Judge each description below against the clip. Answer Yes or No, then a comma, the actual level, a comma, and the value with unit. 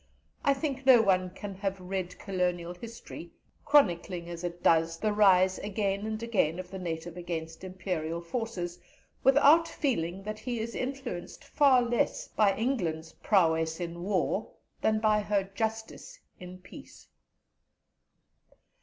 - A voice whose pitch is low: No, high, 195 Hz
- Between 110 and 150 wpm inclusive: Yes, slow, 135 wpm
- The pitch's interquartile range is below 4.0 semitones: No, average, 4.5 semitones